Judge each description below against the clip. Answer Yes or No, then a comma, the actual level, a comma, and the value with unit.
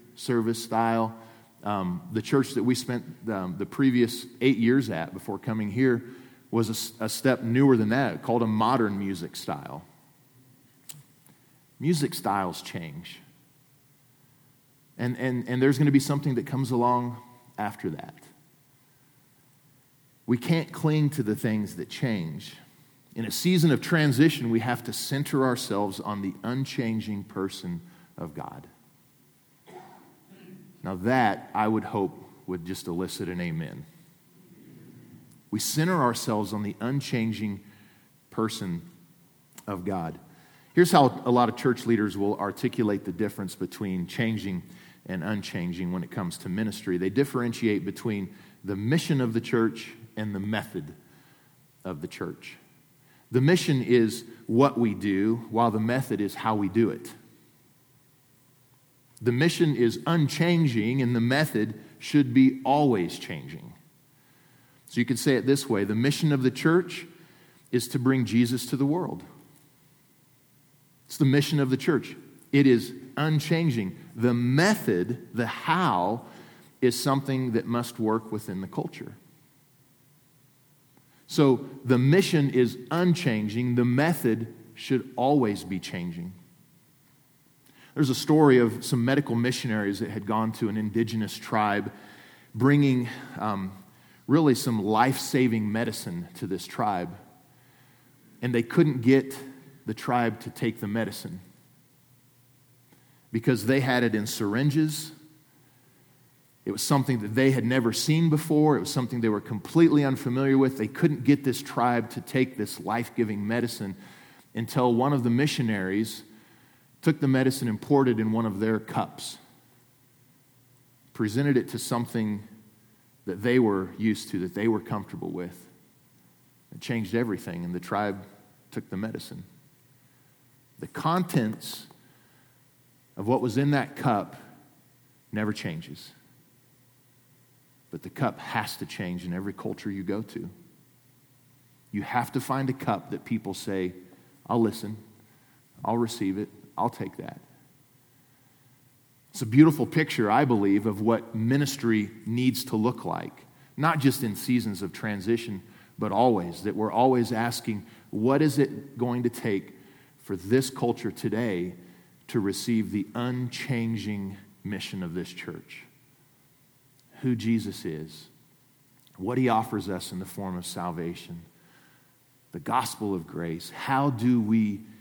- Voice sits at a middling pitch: No, low, 125 Hz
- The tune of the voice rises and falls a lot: No, average, 4.1 semitones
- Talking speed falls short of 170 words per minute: Yes, average, 140 wpm